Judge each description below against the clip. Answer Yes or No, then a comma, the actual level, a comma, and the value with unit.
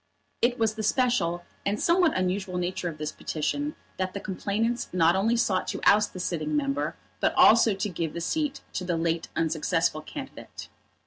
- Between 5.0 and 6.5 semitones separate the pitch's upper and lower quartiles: Yes, average, 5.3 semitones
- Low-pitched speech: No, medium, 185 Hz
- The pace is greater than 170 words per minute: Yes, average, 180 wpm